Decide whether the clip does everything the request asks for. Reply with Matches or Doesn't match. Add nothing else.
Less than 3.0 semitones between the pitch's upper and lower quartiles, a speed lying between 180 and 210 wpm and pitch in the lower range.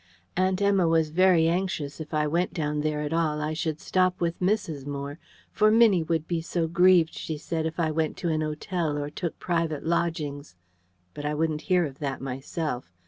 Doesn't match